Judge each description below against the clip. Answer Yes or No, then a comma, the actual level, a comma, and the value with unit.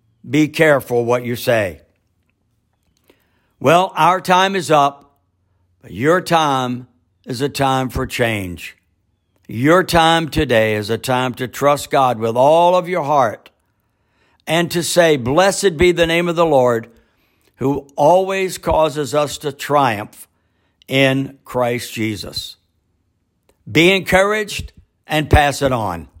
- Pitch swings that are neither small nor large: No, wide, 7.3 semitones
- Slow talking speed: Yes, slow, 130 wpm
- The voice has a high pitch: No, low, 130 Hz